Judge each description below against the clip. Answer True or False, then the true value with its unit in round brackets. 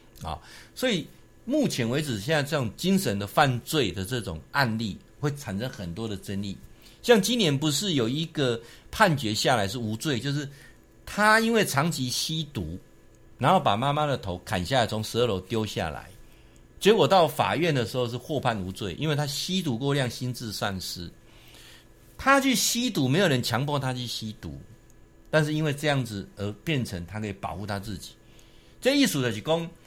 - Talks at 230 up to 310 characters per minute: True (265 characters per minute)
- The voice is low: True (125 Hz)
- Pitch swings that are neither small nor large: False (6.3 semitones)